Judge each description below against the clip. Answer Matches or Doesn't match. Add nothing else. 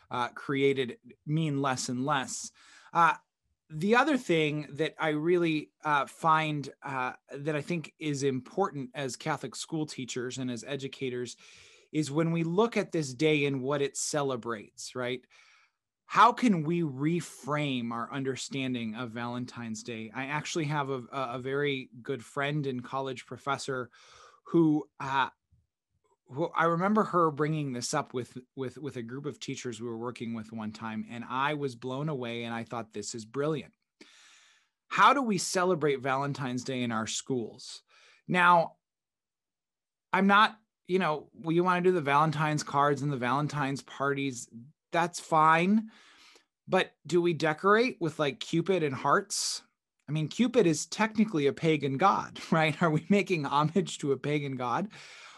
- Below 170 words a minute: Matches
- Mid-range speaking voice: Matches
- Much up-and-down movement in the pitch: Doesn't match